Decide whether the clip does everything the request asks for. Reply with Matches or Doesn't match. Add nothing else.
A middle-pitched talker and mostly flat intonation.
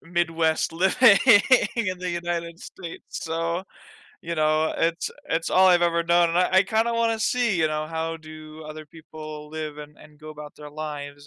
Matches